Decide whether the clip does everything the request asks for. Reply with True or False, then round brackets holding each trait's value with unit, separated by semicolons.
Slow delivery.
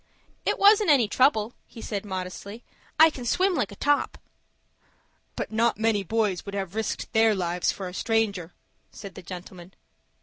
False (165 wpm)